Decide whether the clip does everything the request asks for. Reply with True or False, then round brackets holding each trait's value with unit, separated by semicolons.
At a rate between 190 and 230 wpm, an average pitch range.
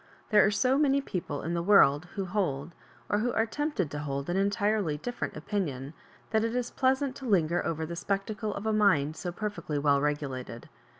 False (200 wpm; 6.5 semitones)